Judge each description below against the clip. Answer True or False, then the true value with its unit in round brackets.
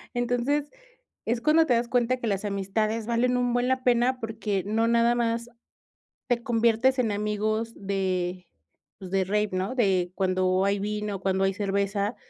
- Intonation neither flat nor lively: True (3.5 semitones)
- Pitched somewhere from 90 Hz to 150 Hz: False (220 Hz)